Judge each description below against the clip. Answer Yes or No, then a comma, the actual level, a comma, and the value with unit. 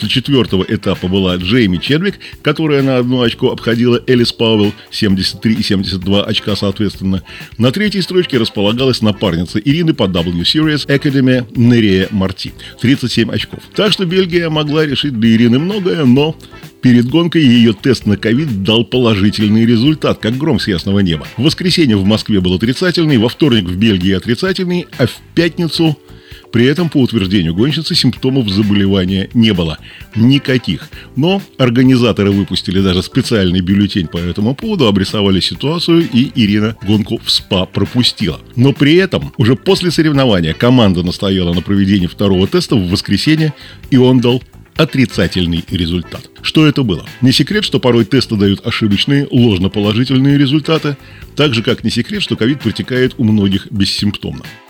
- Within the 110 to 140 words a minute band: No, average, 150 wpm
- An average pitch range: No, wide, 5.9 semitones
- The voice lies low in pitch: Yes, low, 115 Hz